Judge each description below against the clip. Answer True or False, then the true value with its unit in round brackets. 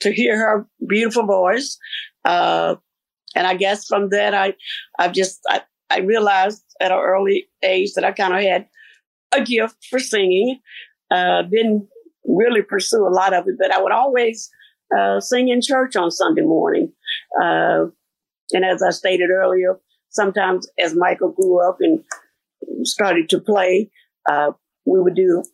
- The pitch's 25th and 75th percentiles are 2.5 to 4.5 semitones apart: False (5.1 semitones)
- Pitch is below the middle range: False (200 Hz)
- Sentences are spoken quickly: False (160 wpm)